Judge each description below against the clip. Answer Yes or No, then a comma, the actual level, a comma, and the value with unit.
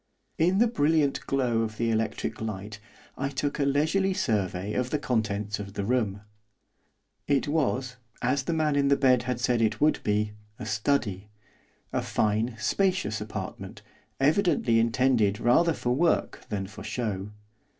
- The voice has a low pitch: Yes, low, 125 Hz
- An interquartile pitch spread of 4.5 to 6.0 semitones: Yes, average, 5.0 semitones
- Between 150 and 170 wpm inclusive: Yes, average, 155 wpm